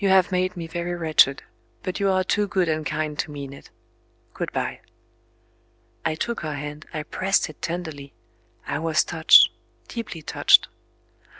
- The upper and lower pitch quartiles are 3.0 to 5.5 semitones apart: Yes, average, 3.3 semitones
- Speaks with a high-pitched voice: No, medium, 165 Hz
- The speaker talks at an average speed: Yes, average, 165 wpm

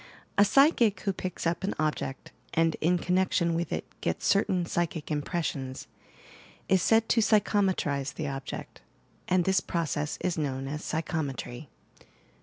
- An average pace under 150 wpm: Yes, average, 140 wpm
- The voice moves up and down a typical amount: Yes, average, 4.2 semitones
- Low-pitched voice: No, medium, 170 Hz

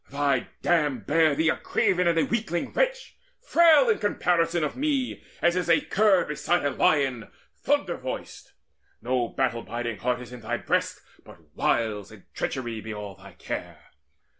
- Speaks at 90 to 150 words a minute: No, average, 165 wpm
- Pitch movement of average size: No, wide, 6.8 semitones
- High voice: No, medium, 150 Hz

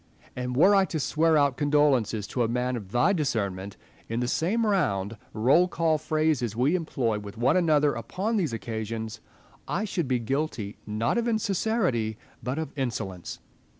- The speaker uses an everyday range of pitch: No, wide, 6.4 semitones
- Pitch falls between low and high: No, low, 130 Hz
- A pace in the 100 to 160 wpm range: No, average, 170 wpm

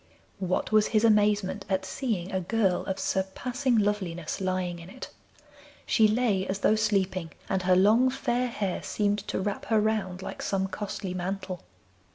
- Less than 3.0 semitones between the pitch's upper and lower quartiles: Yes, narrow, 2.5 semitones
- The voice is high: Yes, high, 200 Hz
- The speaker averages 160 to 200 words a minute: Yes, average, 165 wpm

